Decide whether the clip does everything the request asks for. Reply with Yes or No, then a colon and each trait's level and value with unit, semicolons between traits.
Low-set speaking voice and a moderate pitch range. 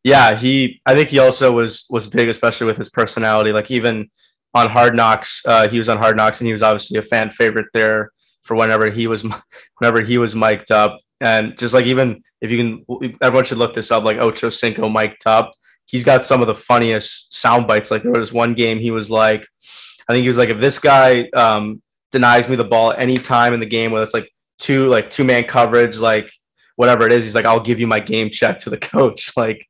No: low, 115 Hz; narrow, 1.7 semitones